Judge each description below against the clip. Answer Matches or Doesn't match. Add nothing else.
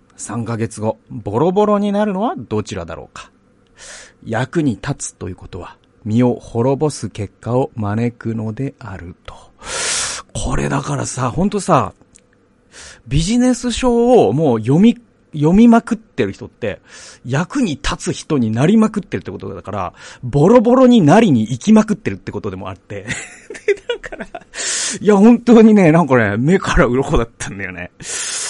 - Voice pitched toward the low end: Matches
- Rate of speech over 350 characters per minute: Doesn't match